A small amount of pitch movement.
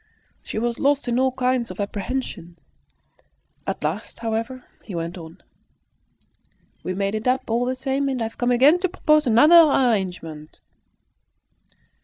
No: average, 4.8 semitones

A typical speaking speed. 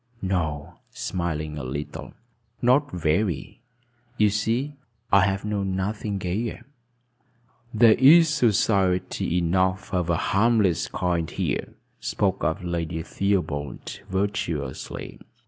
No: slow, 105 wpm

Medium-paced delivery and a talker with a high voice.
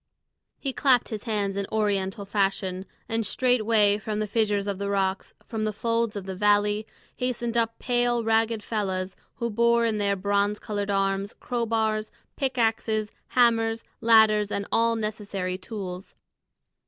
Yes: average, 155 wpm; high, 215 Hz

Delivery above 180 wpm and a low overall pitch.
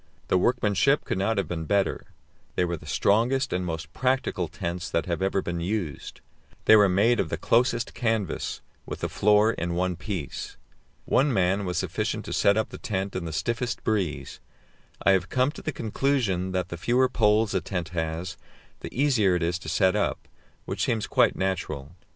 Yes: average, 190 wpm; very low, 95 Hz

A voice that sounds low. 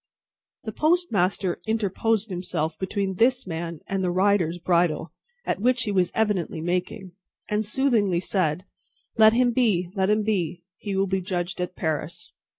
No: high, 190 Hz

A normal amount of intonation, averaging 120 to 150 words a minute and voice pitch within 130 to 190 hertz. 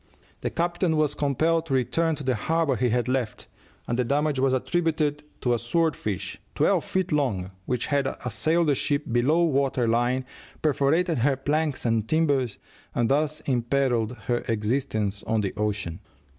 No: average, 4.5 semitones; average, 165 wpm; low, 135 Hz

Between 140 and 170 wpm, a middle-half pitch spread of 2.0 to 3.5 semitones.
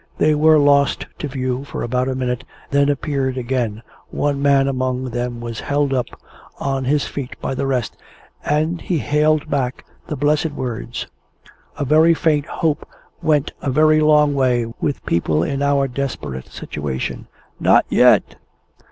Yes: average, 155 wpm; average, 2.7 semitones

